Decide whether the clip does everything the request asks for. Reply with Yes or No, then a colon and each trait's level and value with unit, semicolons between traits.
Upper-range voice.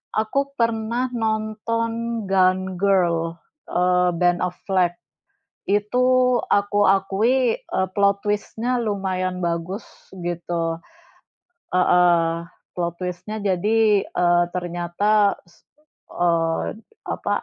Yes: high, 195 Hz